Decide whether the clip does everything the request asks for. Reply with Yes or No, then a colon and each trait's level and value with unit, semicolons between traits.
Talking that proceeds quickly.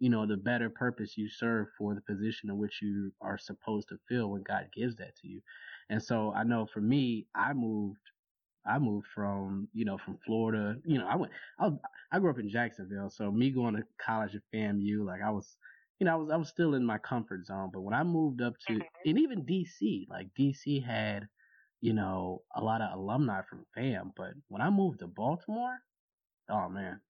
Yes: fast, 215 wpm